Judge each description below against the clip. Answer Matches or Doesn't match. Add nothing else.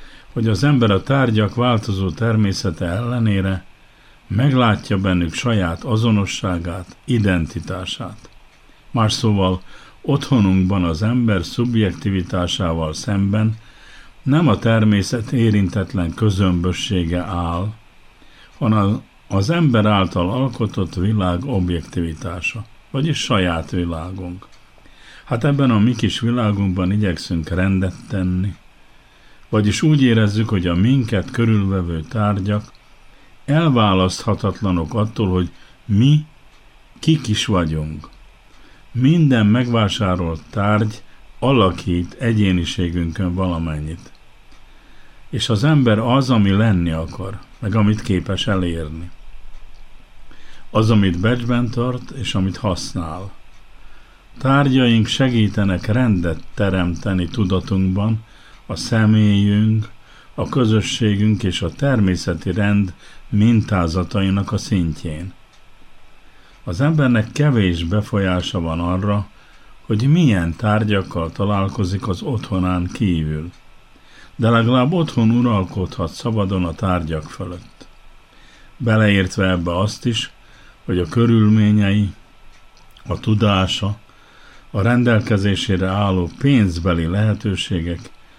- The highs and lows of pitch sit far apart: Doesn't match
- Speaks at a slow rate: Matches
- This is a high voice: Doesn't match